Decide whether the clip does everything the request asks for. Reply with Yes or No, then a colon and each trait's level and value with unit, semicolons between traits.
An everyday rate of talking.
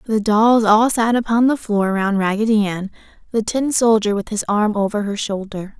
Yes: average, 195 wpm